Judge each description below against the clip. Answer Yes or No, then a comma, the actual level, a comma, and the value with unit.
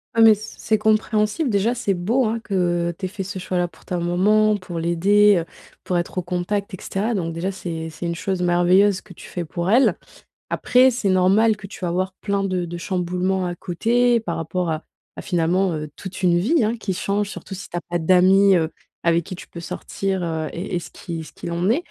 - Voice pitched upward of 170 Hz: Yes, medium, 185 Hz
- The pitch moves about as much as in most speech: Yes, average, 3.0 semitones